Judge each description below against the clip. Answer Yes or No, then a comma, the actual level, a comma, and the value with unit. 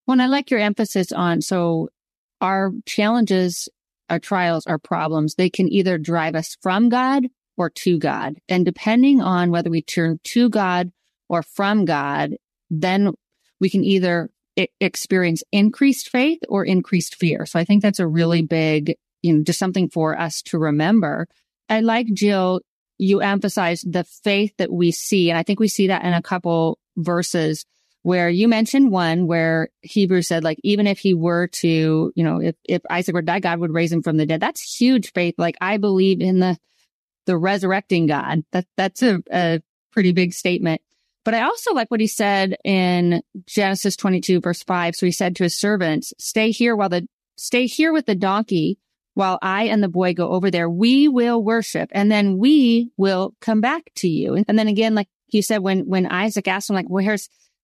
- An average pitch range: Yes, average, 3.4 semitones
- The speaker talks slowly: No, average, 195 wpm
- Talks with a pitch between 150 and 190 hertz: Yes, medium, 185 Hz